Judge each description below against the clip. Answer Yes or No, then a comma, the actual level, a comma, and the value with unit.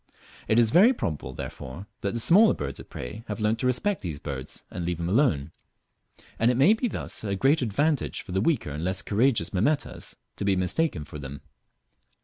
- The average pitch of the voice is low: Yes, low, 105 Hz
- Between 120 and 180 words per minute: No, average, 200 wpm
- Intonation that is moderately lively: No, wide, 8.5 semitones